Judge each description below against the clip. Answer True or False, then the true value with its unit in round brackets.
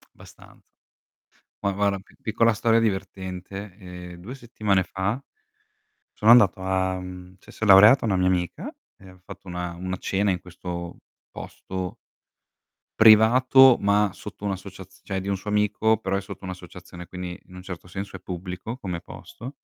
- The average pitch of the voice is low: True (95 Hz)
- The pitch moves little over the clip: True (2.3 semitones)